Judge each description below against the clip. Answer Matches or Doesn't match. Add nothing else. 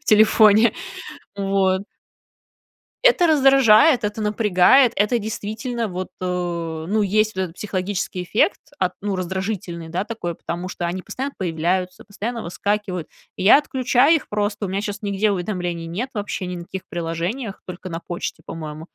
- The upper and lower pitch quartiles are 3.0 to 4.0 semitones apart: Matches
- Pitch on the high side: Matches